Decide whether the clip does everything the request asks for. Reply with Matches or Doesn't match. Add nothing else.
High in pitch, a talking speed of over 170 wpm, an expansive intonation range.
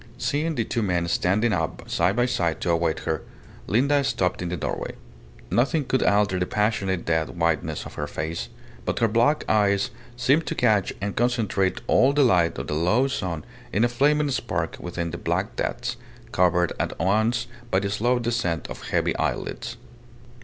Doesn't match